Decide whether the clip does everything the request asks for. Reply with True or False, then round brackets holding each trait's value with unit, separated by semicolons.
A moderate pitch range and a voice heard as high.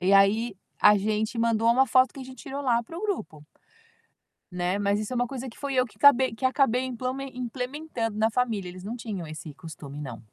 True (4.5 semitones; 230 Hz)